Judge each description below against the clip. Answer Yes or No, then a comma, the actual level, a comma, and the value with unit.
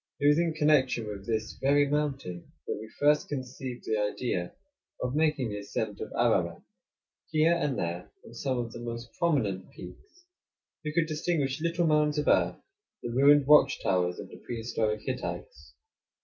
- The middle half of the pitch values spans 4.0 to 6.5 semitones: Yes, average, 5.1 semitones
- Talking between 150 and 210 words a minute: Yes, average, 165 wpm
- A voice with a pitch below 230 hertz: Yes, low, 135 Hz